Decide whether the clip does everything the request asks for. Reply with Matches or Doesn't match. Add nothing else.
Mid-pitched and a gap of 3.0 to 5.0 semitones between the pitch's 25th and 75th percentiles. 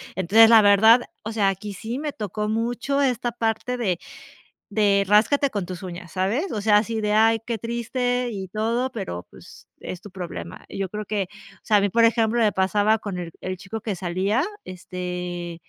Doesn't match